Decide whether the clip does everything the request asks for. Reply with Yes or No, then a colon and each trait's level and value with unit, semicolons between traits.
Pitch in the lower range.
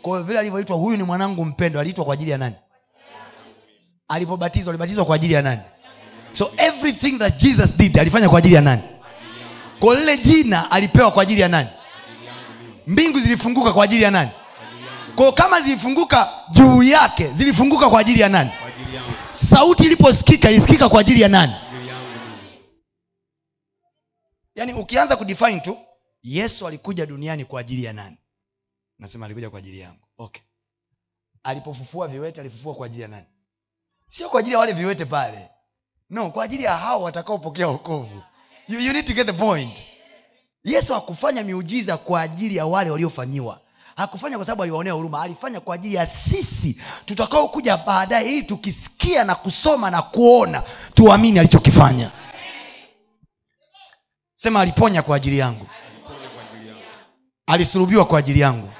No: medium, 170 Hz